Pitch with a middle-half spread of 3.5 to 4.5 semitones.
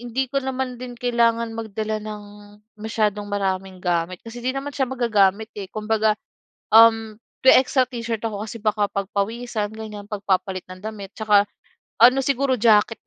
No: average, 2.7 semitones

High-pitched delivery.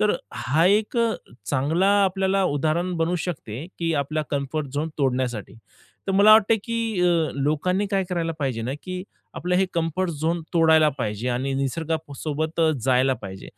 No: medium, 160 Hz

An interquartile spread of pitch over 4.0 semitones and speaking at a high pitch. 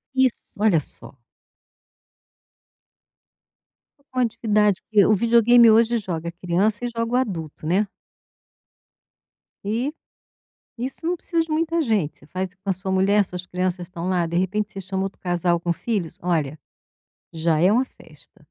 Yes: average, 4.6 semitones; high, 195 Hz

